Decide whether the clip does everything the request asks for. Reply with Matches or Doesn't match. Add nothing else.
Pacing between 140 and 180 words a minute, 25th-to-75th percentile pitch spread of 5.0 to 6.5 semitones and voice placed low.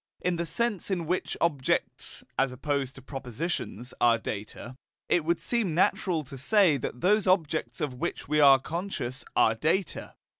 Doesn't match